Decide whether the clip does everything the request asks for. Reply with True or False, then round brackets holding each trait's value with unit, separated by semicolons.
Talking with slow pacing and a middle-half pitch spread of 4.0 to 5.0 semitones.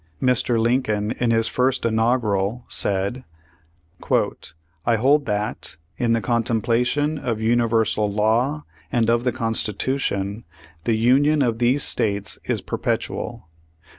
False (115 wpm; 2.7 semitones)